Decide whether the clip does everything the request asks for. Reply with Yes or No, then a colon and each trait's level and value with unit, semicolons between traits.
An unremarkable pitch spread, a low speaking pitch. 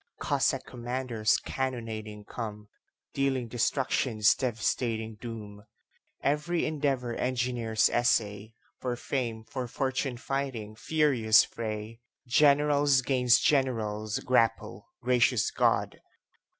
Yes: average, 3.2 semitones; low, 120 Hz